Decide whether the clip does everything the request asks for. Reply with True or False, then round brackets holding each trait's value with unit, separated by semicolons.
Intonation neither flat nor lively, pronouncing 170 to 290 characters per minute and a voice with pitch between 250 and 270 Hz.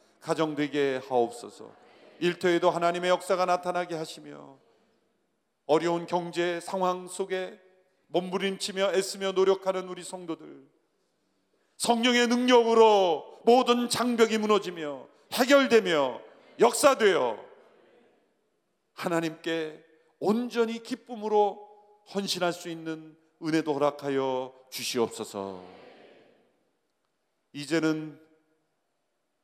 False (4.7 semitones; 220 characters per minute; 180 Hz)